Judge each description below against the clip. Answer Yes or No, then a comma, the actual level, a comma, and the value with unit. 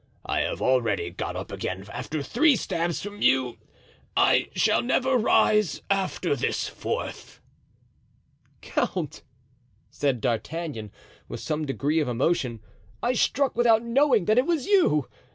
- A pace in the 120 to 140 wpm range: Yes, slow, 135 wpm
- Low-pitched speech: No, medium, 170 Hz